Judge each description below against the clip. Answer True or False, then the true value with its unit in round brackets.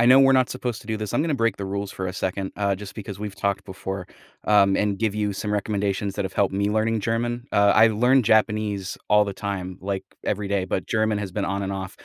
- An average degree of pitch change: False (1.9 semitones)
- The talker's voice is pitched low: True (100 Hz)